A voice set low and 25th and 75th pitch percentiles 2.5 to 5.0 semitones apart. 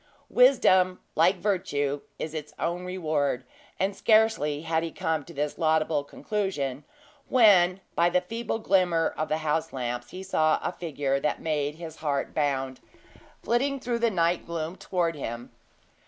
No: medium, 165 Hz; average, 4.0 semitones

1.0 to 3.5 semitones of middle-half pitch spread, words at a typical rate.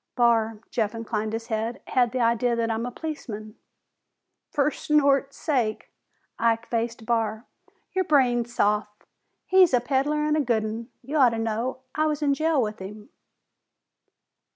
No: average, 3.9 semitones; average, 155 wpm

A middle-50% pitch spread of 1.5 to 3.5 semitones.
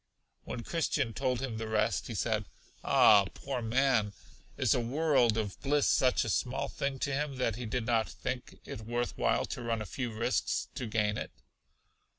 Yes: average, 3.1 semitones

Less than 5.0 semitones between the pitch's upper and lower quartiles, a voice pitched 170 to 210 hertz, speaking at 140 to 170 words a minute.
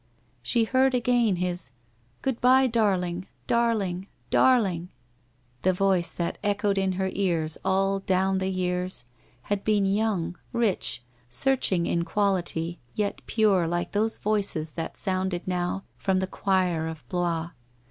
Yes: average, 3.1 semitones; high, 190 Hz; average, 150 wpm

